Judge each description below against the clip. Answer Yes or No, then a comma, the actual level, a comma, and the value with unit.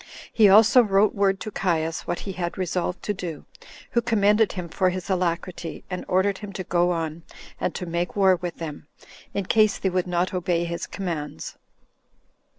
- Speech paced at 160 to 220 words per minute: Yes, average, 180 wpm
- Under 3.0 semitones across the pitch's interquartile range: Yes, narrow, 2.5 semitones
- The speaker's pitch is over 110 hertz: Yes, medium, 185 Hz